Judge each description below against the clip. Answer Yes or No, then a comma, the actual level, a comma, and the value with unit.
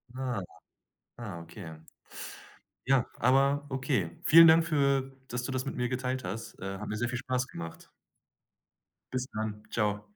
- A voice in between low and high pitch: No, low, 125 Hz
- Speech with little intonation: No, average, 4.1 semitones